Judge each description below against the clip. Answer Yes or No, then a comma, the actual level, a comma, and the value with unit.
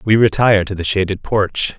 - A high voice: No, low, 100 Hz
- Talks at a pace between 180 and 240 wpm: Yes, average, 200 wpm